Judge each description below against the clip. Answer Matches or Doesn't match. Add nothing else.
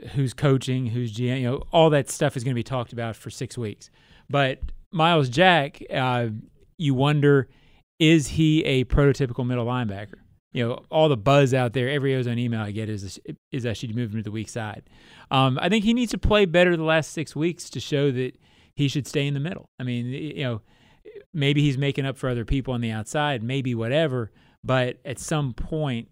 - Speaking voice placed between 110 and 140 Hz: Matches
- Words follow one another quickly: Matches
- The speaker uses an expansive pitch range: Doesn't match